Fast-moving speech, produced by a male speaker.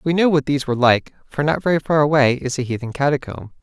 Yes: fast, 250 wpm; male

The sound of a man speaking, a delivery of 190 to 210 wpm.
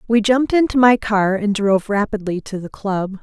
No: female; fast, 205 wpm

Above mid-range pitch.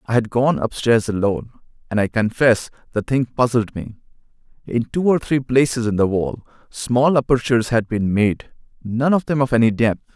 No: low, 120 Hz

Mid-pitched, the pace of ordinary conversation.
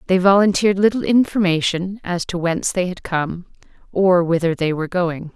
Yes: medium, 180 Hz; average, 170 wpm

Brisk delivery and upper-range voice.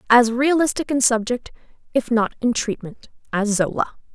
No: average, 145 wpm; high, 240 Hz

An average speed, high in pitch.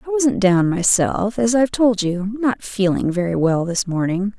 Yes: average, 180 wpm; high, 205 Hz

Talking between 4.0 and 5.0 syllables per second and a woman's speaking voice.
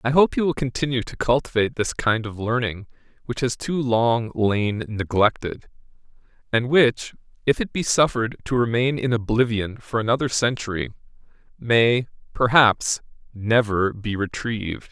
No: 4.7 syllables/s; male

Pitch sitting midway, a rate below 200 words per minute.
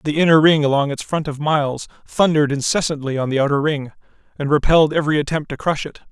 No: medium, 150 Hz; fast, 205 wpm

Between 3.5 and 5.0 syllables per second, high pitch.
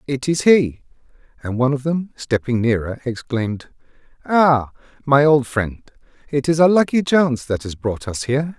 No: 4.9 syllables/s; low, 135 Hz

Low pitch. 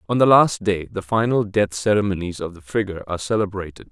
Yes: low, 100 Hz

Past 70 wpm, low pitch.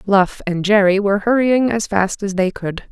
No: fast, 205 wpm; high, 200 Hz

